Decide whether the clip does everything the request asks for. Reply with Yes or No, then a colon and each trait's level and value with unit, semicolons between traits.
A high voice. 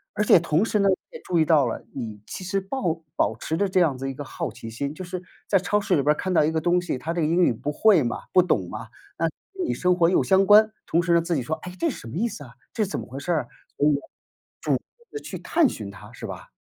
No: medium, 170 Hz